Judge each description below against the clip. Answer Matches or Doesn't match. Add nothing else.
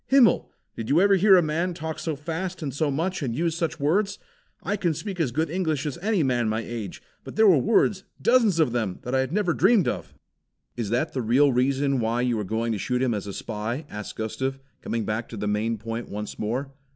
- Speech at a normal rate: Doesn't match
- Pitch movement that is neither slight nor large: Doesn't match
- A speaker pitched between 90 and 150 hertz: Matches